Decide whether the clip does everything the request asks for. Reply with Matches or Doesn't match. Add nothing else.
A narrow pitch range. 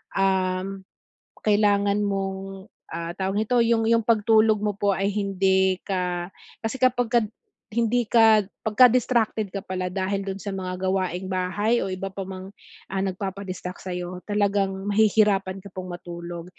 Matches